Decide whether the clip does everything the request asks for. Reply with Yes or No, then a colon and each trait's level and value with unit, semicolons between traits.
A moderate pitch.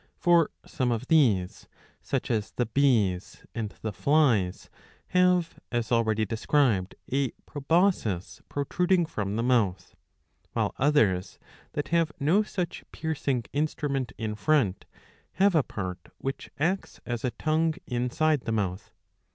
No: low, 130 Hz